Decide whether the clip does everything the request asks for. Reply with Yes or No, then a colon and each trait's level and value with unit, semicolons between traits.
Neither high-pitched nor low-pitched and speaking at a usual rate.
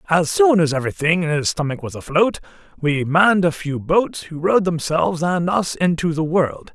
Yes: medium, 165 Hz; average, 195 wpm